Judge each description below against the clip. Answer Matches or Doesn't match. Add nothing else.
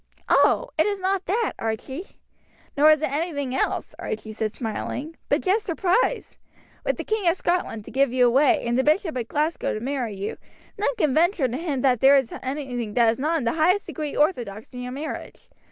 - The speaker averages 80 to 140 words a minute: Doesn't match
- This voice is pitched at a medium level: Doesn't match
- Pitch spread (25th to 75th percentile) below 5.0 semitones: Doesn't match